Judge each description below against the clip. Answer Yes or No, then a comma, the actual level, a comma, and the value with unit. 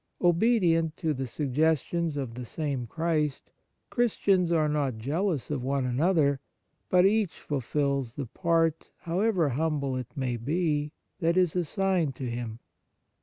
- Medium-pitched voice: Yes, medium, 150 Hz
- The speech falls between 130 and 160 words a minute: Yes, average, 140 wpm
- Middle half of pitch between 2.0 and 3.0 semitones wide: No, average, 4.1 semitones